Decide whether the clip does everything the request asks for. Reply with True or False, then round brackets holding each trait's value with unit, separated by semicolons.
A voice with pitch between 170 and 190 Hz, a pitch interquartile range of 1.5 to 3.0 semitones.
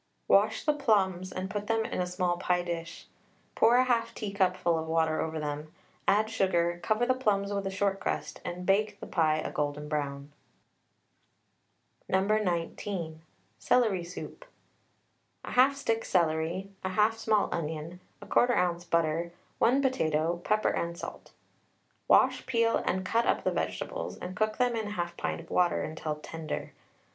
False (185 Hz; 4.5 semitones)